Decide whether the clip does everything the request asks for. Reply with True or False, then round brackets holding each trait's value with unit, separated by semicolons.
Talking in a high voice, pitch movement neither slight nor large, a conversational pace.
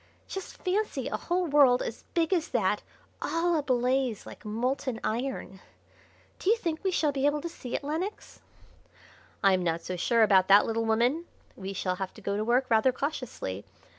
False (250 Hz; 6.8 semitones; 180 wpm)